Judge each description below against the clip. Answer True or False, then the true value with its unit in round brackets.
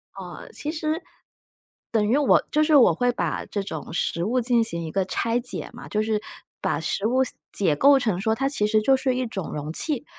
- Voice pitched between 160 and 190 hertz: False (230 Hz)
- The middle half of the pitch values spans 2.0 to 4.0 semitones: False (5.2 semitones)